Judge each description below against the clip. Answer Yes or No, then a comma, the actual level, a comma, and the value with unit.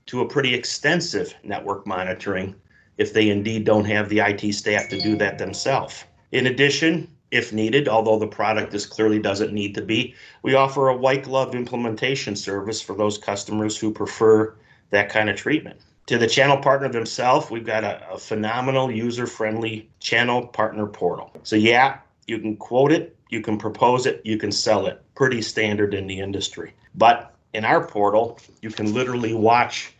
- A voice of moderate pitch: No, low, 110 Hz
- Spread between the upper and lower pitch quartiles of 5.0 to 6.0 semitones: No, average, 3.2 semitones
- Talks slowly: No, average, 175 wpm